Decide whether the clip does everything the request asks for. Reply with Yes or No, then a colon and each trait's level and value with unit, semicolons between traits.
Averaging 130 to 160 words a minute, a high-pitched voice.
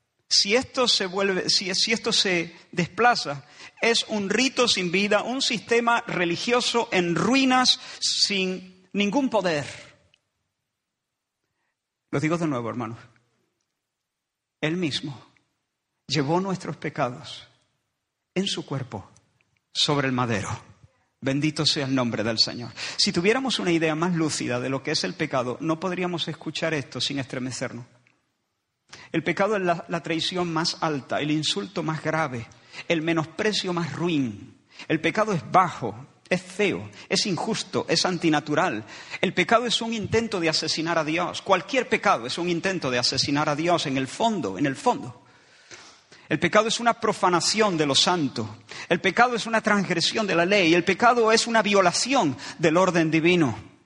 No: average, 150 wpm; medium, 170 Hz